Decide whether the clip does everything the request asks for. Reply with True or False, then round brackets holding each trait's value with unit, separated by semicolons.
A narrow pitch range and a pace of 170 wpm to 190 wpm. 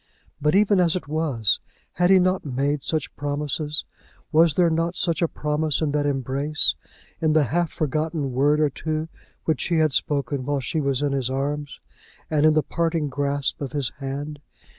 True (2.2 semitones; 185 wpm)